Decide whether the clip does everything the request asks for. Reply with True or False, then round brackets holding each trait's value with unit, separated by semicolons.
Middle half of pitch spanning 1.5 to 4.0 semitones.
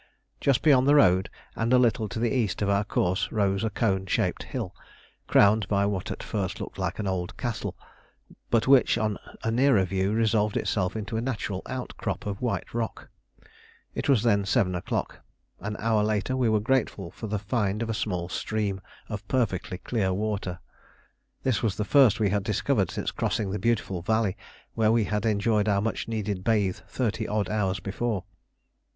True (2.6 semitones)